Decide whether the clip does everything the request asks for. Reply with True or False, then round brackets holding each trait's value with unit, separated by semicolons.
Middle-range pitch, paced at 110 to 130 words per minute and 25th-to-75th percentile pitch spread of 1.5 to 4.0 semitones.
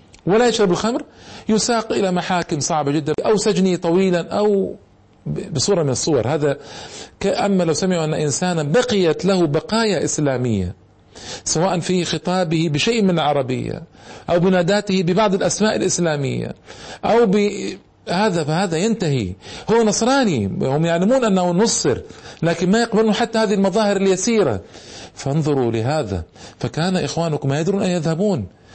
False (180 Hz; 125 wpm; 5.0 semitones)